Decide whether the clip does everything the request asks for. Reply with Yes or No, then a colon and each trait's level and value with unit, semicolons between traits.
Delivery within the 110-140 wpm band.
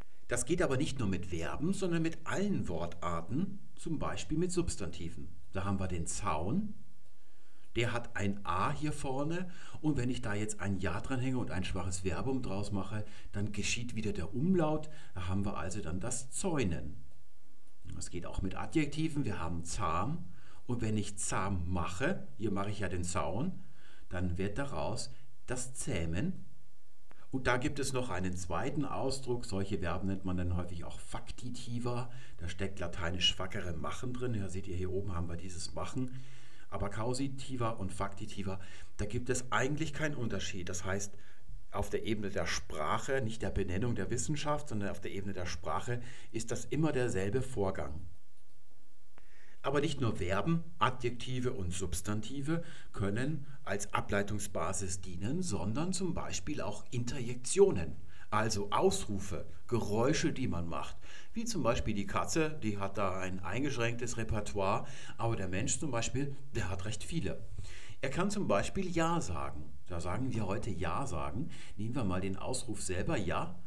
No: average, 165 wpm